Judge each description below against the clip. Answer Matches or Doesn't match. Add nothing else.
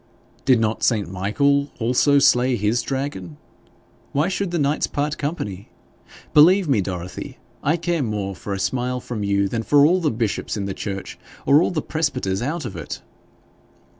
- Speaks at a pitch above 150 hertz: Doesn't match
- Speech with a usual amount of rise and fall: Doesn't match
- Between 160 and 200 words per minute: Matches